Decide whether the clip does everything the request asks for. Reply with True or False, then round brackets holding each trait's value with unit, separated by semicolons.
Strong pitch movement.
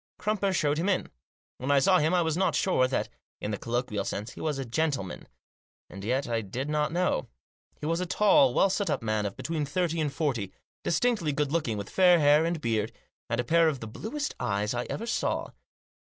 True (6.8 semitones)